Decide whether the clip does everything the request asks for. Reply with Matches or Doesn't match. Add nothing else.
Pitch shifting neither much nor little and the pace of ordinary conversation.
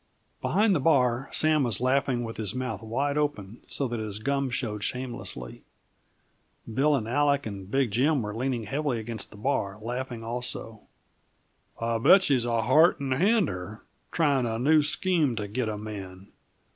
Matches